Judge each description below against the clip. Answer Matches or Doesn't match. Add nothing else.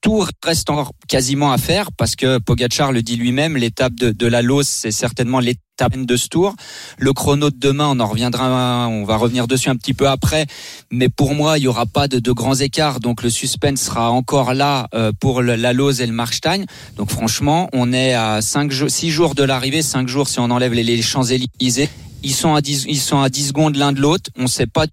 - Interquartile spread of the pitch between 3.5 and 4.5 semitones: Doesn't match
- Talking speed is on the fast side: Matches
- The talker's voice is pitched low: Matches